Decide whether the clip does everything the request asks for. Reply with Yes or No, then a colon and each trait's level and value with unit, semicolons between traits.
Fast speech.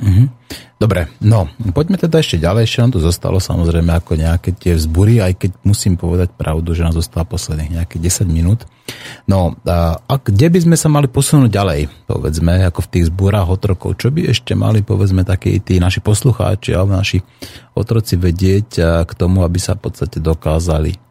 Yes: fast, 175 wpm